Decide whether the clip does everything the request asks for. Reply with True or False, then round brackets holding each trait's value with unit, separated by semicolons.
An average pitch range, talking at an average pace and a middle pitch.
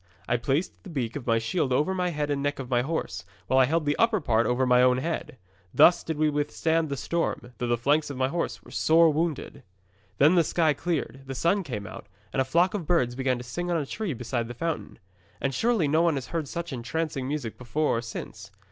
False (4.8 semitones; 235 wpm; 145 Hz)